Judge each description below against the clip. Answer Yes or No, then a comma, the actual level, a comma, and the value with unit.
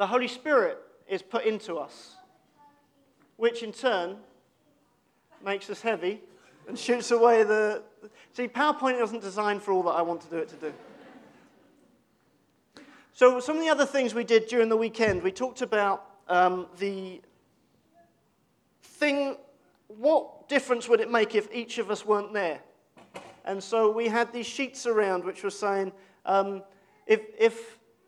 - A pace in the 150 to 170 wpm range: Yes, average, 155 wpm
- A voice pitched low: No, high, 230 Hz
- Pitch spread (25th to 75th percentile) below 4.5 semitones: No, average, 5.3 semitones